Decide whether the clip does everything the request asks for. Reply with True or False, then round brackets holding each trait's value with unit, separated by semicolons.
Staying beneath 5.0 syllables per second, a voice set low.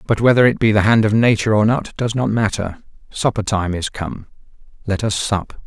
False (5.5 syllables/s; 105 Hz)